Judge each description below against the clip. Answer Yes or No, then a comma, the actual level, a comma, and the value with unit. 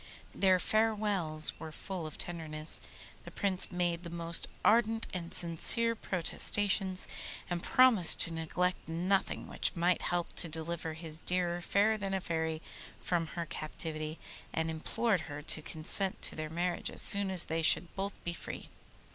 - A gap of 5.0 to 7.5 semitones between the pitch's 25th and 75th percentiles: No, average, 3.1 semitones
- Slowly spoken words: No, average, 155 wpm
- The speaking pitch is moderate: Yes, medium, 175 Hz